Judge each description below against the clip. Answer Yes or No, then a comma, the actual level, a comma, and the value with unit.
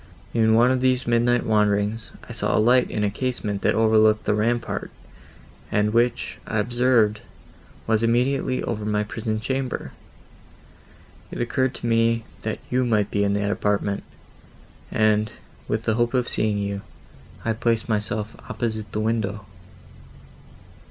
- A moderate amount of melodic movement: No, narrow, 2.1 semitones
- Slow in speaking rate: No, average, 145 wpm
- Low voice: Yes, low, 110 Hz